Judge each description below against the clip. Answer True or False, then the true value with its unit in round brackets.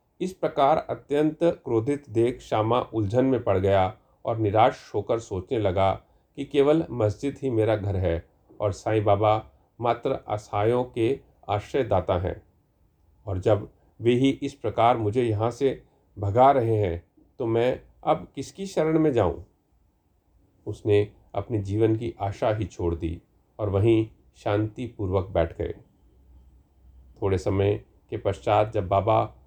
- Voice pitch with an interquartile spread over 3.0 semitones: True (3.9 semitones)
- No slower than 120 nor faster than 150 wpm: True (140 wpm)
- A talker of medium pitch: False (105 Hz)